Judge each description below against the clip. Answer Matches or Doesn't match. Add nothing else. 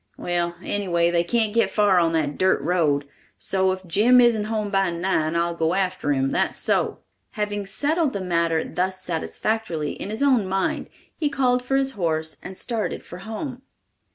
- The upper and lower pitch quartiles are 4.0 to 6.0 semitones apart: Matches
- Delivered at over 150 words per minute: Matches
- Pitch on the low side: Doesn't match